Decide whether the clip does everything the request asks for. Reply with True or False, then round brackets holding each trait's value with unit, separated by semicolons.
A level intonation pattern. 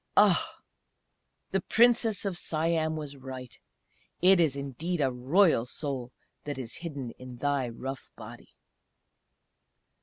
False (4.8 semitones)